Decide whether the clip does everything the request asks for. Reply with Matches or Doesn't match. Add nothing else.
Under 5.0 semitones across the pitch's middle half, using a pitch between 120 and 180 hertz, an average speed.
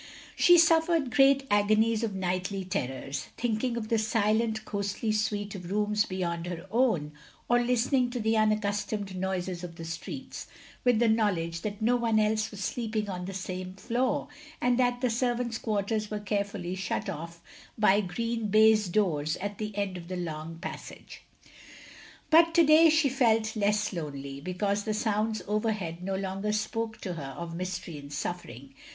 Doesn't match